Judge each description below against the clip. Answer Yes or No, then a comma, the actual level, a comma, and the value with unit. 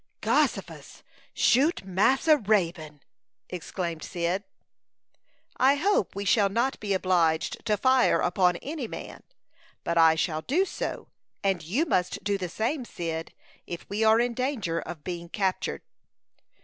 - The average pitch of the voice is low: No, high, 195 Hz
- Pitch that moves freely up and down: Yes, wide, 6.0 semitones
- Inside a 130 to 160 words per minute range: Yes, slow, 135 wpm